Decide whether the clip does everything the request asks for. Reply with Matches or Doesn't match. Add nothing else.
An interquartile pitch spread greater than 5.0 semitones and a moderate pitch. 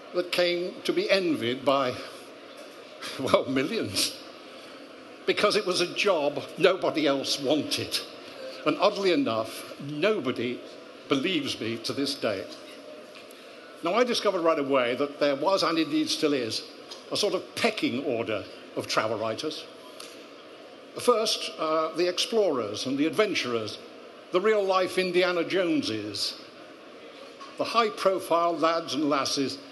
Matches